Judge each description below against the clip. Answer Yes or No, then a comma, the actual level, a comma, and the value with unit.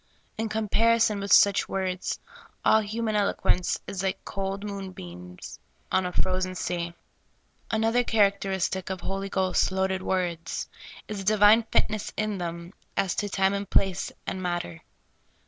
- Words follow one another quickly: No, average, 140 wpm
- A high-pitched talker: Yes, high, 195 Hz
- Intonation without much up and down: Yes, narrow, 2.1 semitones